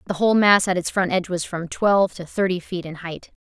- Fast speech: Yes, fast, 260 wpm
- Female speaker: Yes, female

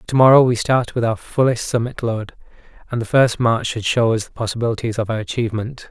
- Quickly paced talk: Yes, fast, 215 wpm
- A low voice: Yes, low, 115 Hz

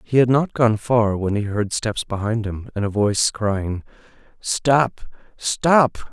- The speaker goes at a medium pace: Yes, average, 165 wpm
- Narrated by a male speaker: Yes, male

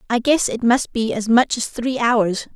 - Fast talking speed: Yes, fast, 235 wpm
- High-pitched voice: Yes, high, 235 Hz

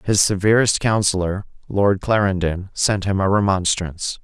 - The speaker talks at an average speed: No, slow, 125 wpm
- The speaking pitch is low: Yes, very low, 95 Hz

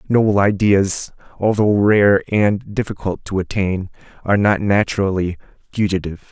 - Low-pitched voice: Yes, low, 100 Hz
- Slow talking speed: Yes, slow, 115 wpm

